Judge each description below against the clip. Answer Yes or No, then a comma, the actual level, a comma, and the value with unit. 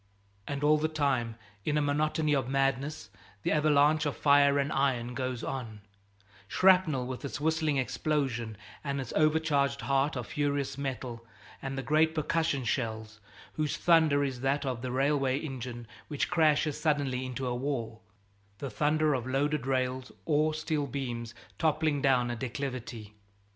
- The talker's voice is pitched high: No, medium, 140 Hz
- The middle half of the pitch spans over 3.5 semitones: No, average, 3.0 semitones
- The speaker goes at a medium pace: Yes, average, 155 wpm